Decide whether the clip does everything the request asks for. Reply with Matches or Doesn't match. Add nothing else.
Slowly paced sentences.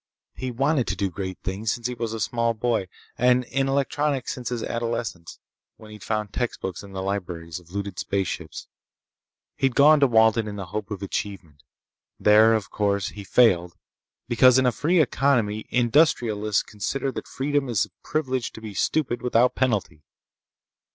Doesn't match